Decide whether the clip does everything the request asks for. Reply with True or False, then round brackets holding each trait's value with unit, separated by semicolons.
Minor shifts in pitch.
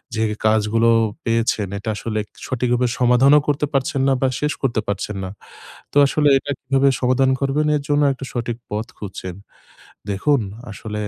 False (3.9 semitones)